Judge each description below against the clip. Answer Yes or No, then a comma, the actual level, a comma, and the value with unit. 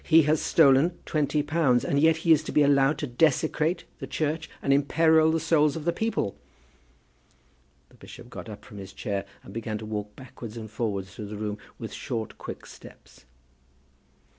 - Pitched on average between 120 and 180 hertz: Yes, medium, 140 Hz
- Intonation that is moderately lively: No, wide, 6.5 semitones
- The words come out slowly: No, average, 185 wpm